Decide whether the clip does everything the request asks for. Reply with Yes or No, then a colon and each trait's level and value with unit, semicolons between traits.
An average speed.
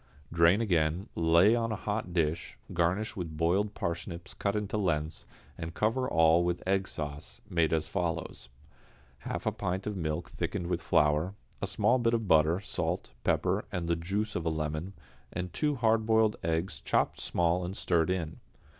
Yes: average, 170 wpm